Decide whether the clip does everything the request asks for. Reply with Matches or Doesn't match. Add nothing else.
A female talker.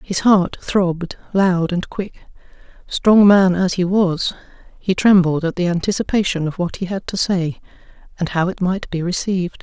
Matches